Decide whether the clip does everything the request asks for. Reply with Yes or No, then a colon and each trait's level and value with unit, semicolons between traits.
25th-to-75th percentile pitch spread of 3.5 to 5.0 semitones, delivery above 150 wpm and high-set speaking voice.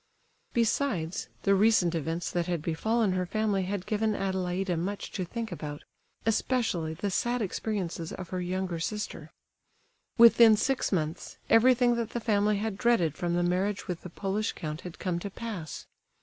Yes: average, 4.0 semitones; average, 165 wpm; high, 195 Hz